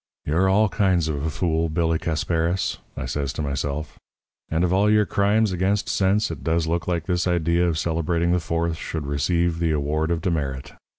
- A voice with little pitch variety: Yes, narrow, 2.3 semitones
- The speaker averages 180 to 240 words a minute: Yes, average, 190 wpm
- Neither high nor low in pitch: No, very low, 85 Hz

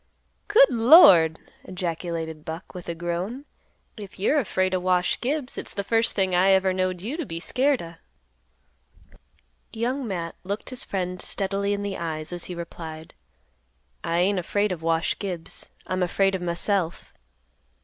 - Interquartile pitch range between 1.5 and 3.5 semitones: Yes, average, 3.1 semitones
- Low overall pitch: No, medium, 185 Hz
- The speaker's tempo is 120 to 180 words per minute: Yes, average, 160 wpm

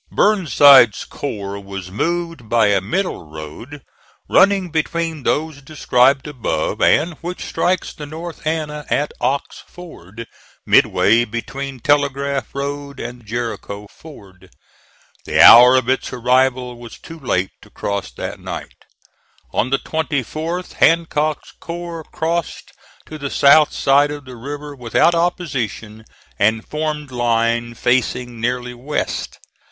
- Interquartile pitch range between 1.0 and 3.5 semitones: No, average, 4.8 semitones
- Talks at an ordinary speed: No, slow, 125 wpm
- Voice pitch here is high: No, low, 135 Hz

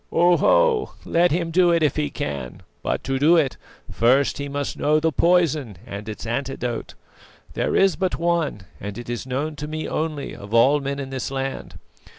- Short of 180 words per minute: No, average, 185 wpm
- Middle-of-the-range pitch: Yes, medium, 145 Hz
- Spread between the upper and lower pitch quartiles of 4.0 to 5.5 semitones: Yes, average, 4.7 semitones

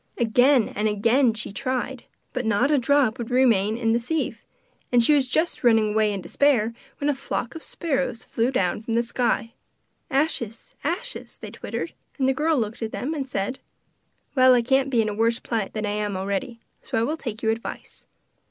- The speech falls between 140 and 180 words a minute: No, average, 200 wpm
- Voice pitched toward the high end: Yes, high, 240 Hz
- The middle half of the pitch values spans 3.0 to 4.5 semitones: Yes, average, 3.5 semitones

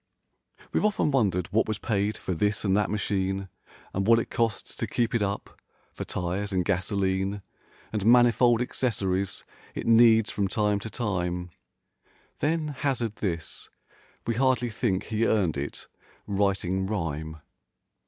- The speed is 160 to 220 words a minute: No, average, 145 wpm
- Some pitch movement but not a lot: Yes, average, 3.3 semitones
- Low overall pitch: Yes, low, 105 Hz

